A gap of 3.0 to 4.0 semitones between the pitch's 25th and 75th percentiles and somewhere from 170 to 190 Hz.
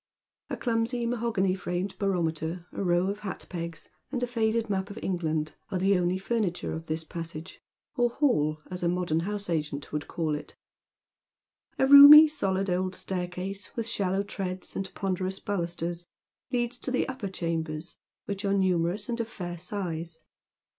Yes: average, 3.5 semitones; medium, 185 Hz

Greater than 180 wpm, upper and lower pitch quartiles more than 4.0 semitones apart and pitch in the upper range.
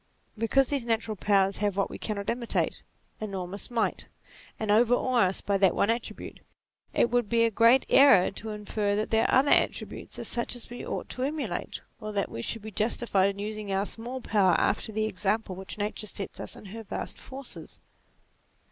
No: average, 190 wpm; average, 2.9 semitones; high, 215 Hz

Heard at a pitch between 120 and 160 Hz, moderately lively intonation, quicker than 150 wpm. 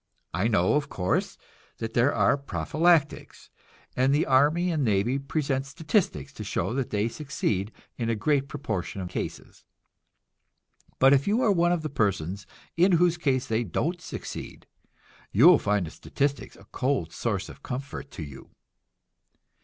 No: low, 135 Hz; wide, 6.5 semitones; average, 160 wpm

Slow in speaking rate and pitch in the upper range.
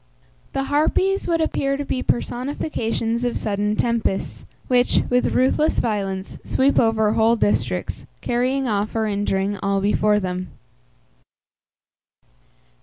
Yes: slow, 115 wpm; high, 225 Hz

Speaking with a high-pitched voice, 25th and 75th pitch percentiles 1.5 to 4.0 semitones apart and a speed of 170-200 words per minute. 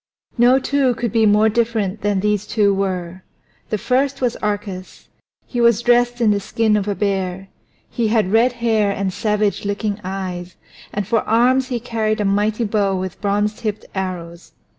Yes: high, 210 Hz; average, 3.0 semitones; average, 175 wpm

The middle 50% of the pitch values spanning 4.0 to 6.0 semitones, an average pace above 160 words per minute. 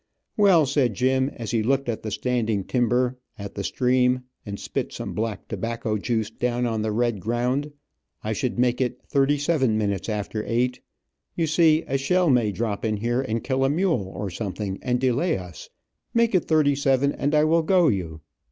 Yes: average, 4.3 semitones; average, 190 wpm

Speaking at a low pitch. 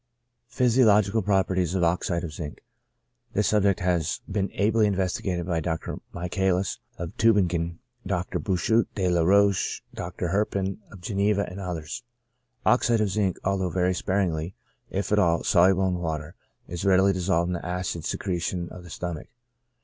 Yes: very low, 95 Hz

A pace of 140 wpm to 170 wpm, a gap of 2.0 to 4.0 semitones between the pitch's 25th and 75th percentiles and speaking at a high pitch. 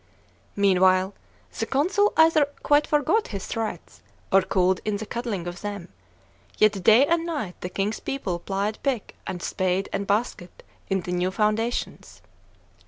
No: average, 150 wpm; average, 4.8 semitones; high, 205 Hz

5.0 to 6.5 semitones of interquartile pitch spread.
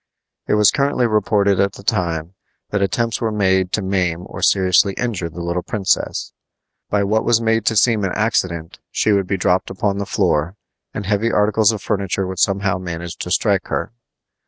No: average, 2.7 semitones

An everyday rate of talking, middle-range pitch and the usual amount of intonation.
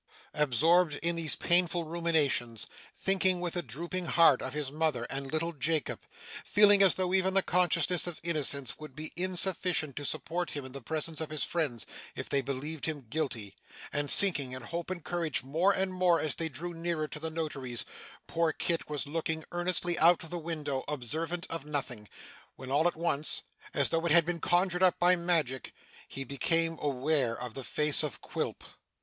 Yes: average, 185 wpm; medium, 160 Hz; average, 3.5 semitones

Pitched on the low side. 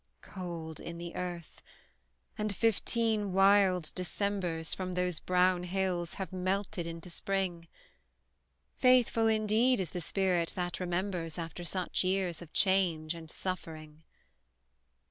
No: medium, 180 Hz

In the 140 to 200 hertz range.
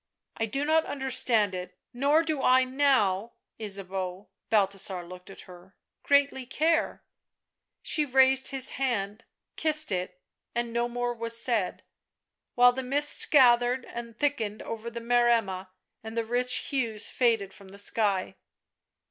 No: high, 235 Hz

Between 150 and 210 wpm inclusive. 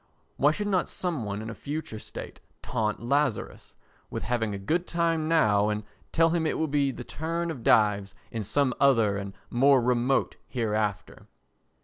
Yes: average, 170 wpm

